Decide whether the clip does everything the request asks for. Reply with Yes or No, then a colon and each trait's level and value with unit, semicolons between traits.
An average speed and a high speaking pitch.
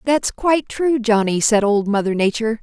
Yes: average, 185 wpm; high, 230 Hz